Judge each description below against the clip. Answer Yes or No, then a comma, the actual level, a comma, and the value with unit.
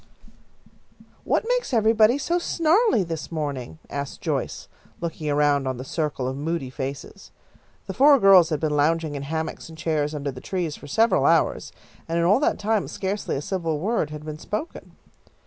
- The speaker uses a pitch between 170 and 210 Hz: No, medium, 160 Hz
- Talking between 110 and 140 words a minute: No, average, 175 wpm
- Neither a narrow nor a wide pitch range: No, wide, 6.2 semitones